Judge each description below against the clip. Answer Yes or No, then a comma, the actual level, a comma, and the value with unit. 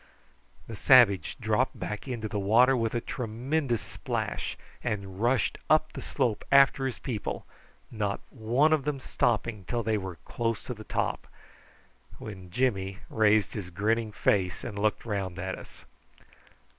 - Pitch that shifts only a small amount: No, average, 3.5 semitones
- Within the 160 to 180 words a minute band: No, average, 150 wpm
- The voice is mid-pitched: No, low, 110 Hz